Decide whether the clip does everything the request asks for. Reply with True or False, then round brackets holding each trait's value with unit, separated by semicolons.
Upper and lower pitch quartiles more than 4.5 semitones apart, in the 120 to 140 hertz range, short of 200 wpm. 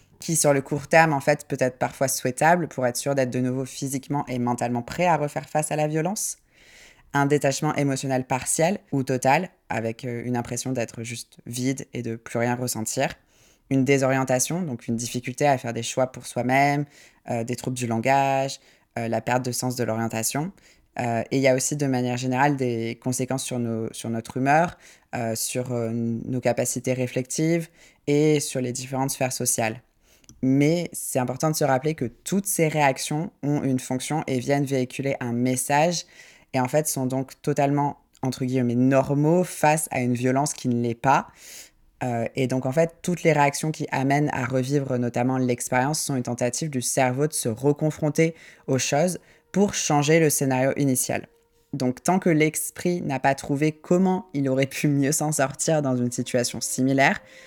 False (3.1 semitones; 135 Hz; 185 wpm)